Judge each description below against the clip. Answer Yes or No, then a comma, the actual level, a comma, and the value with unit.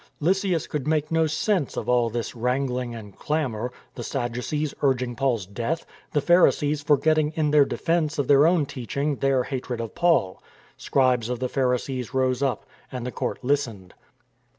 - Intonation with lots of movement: No, average, 3.5 semitones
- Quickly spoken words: No, average, 175 wpm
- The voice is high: No, low, 135 Hz